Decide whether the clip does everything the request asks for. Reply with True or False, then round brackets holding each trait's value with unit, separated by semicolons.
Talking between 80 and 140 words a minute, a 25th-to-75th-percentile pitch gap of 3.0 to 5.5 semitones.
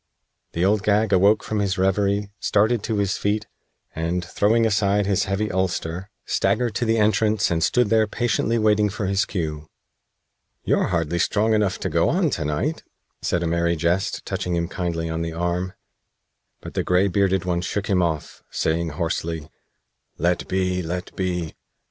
False (170 wpm; 3.4 semitones)